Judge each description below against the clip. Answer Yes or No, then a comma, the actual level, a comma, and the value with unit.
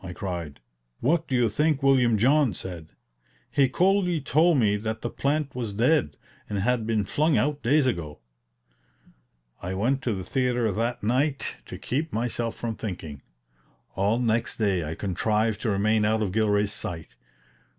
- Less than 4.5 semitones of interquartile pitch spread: No, average, 5.0 semitones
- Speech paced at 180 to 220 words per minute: No, average, 160 wpm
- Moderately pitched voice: No, low, 115 Hz